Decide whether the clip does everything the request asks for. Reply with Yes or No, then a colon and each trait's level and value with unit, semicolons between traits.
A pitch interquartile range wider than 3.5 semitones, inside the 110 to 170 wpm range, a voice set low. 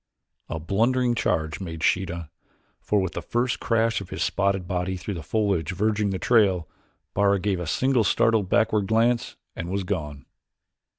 Yes: average, 3.9 semitones; average, 165 wpm; low, 100 Hz